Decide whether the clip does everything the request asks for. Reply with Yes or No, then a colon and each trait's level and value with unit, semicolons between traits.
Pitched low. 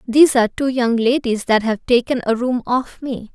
No: high, 245 Hz